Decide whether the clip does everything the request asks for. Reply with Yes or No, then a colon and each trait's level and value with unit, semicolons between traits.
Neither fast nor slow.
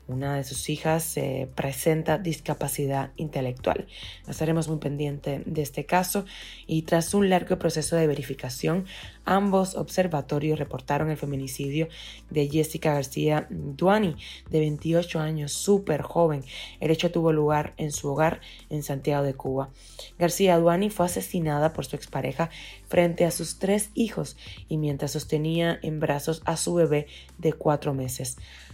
Yes: average, 145 wpm